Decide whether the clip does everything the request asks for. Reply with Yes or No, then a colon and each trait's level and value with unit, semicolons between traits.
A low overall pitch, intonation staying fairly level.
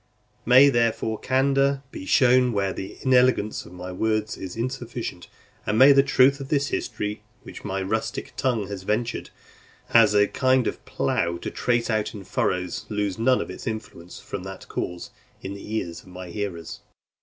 No: low, 110 Hz; average, 4.8 semitones